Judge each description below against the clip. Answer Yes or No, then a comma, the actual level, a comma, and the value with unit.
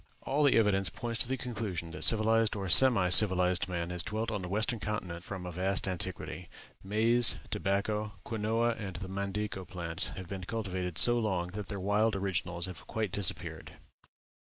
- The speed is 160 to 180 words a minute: Yes, average, 175 wpm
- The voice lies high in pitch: No, low, 100 Hz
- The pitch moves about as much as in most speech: Yes, average, 3.3 semitones